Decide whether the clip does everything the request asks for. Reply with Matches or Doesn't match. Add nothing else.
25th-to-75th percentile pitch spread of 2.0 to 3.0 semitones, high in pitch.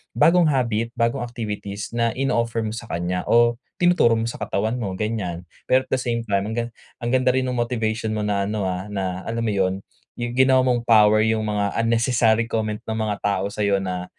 Doesn't match